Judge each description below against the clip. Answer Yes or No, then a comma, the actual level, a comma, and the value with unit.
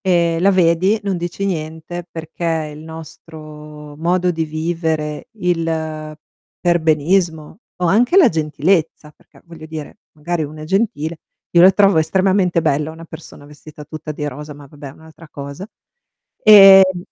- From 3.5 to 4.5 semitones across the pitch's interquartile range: No, narrow, 2.6 semitones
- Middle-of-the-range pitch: Yes, medium, 160 Hz